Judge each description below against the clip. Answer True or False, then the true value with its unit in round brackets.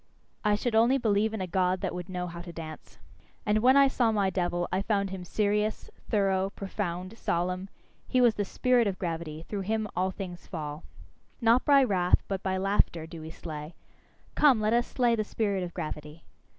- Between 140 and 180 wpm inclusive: False (195 wpm)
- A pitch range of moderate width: True (3.7 semitones)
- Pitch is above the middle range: True (195 Hz)